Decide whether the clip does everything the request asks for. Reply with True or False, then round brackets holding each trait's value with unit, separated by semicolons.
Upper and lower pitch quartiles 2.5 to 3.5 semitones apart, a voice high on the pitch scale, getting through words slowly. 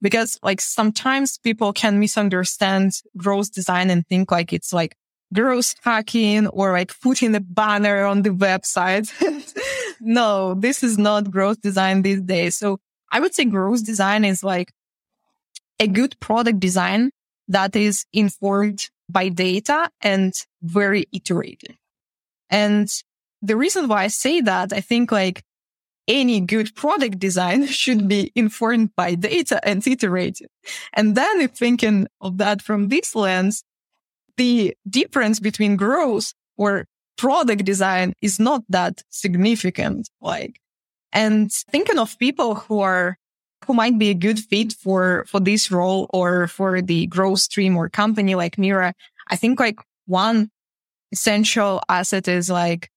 False (3.0 semitones; 205 Hz; 145 wpm)